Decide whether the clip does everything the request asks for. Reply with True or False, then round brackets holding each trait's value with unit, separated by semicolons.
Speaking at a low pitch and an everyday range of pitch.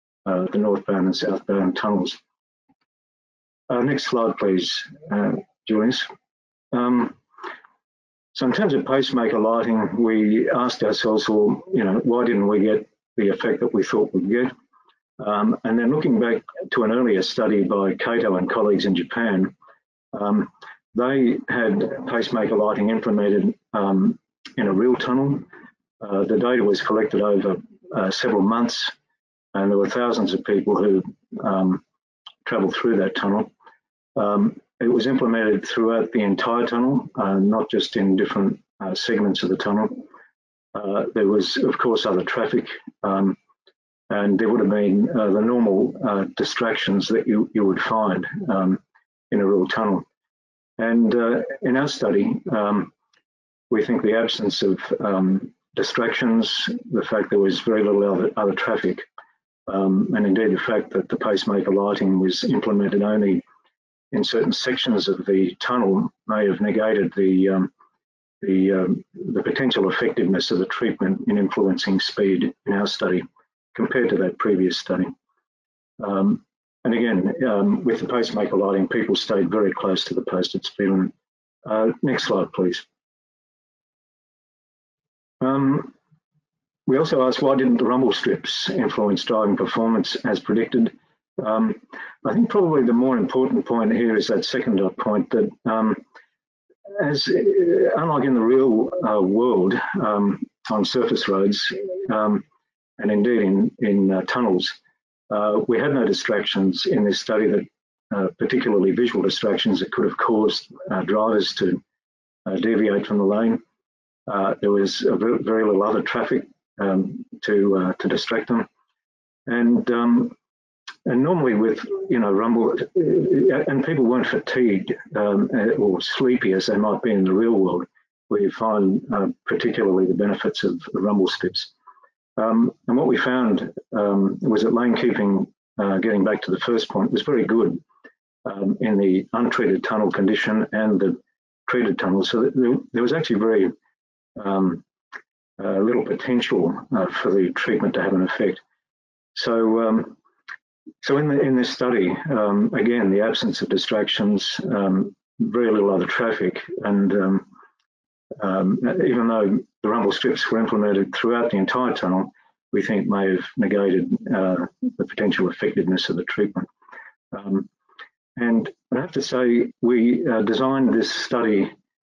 True (105 Hz; 3.9 semitones)